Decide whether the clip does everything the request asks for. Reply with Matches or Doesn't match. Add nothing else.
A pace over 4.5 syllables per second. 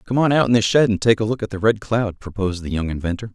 Matches